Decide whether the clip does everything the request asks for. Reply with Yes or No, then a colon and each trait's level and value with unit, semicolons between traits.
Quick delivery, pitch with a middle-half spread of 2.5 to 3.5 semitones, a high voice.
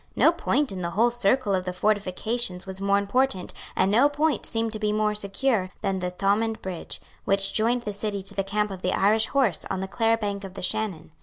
Yes: fast, 225 wpm; average, 2.8 semitones; high, 205 Hz